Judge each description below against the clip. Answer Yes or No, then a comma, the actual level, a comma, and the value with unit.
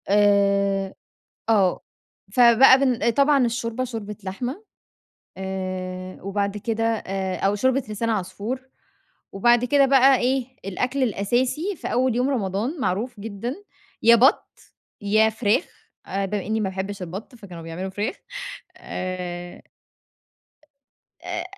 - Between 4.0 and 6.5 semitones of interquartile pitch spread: Yes, average, 4.4 semitones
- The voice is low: No, high, 215 Hz